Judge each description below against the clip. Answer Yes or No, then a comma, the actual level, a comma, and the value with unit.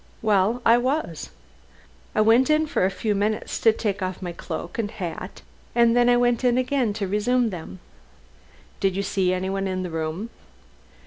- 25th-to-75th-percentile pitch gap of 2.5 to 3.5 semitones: No, average, 4.4 semitones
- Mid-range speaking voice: No, high, 210 Hz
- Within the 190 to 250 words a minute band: No, average, 180 wpm